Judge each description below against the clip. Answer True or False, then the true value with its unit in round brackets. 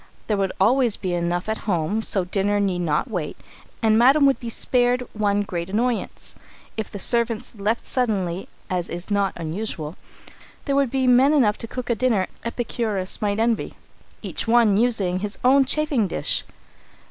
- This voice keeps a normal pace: True (170 wpm)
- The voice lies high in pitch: True (215 Hz)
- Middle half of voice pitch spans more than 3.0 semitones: True (4.2 semitones)